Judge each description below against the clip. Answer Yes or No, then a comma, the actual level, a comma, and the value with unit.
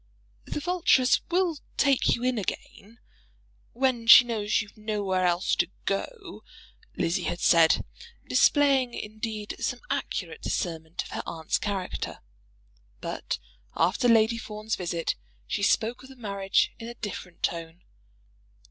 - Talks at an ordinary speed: No, slow, 130 wpm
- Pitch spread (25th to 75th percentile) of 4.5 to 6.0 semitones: Yes, wide, 5.4 semitones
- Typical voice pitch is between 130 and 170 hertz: No, high, 215 Hz